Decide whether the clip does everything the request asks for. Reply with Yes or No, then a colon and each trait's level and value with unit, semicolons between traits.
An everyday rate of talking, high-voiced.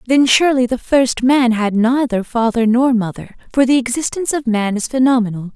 Yes: average, 185 wpm; high, 245 Hz